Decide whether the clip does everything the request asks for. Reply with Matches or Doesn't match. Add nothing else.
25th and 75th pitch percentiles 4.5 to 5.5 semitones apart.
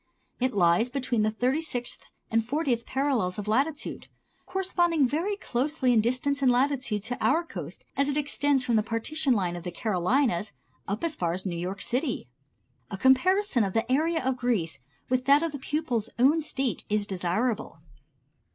Matches